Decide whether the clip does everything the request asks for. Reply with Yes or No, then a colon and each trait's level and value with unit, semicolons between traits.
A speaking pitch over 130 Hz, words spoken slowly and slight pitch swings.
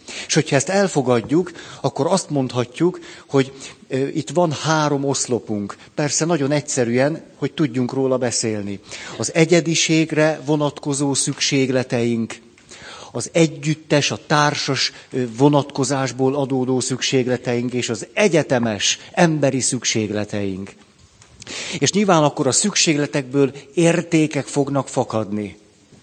No: medium, 140 Hz; slow, 100 wpm; average, 3.5 semitones